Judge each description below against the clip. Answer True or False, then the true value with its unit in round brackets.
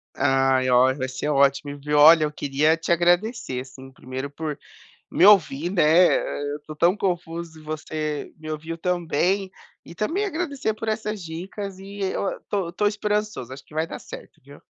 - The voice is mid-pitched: True (165 Hz)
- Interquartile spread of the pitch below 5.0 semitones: False (5.4 semitones)